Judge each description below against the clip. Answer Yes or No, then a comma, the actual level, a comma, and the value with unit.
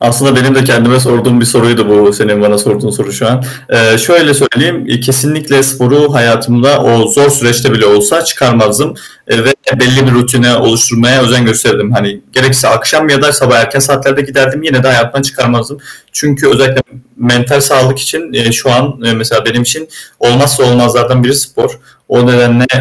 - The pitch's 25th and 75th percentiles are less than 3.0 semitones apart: Yes, narrow, 2.6 semitones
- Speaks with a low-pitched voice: Yes, low, 125 Hz